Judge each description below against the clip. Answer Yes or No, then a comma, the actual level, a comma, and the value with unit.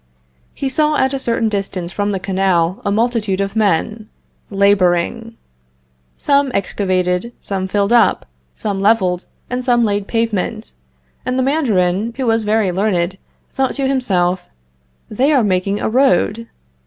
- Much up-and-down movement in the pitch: No, average, 3.9 semitones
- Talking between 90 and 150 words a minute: Yes, average, 140 wpm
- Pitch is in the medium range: No, high, 210 Hz